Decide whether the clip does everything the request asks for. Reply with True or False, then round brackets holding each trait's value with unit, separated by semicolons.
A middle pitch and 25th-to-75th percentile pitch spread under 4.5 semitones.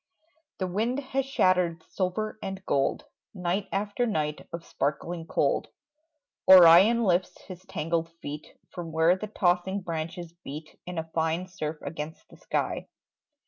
True (175 Hz; 3.0 semitones)